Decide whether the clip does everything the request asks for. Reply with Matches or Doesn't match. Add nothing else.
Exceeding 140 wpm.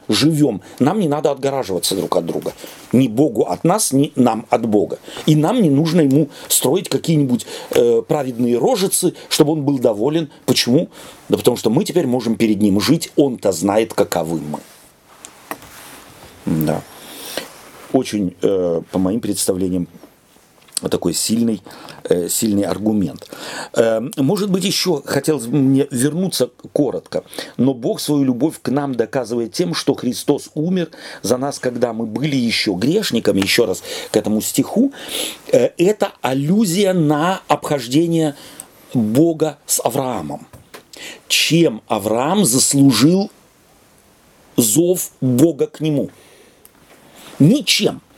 Doesn't match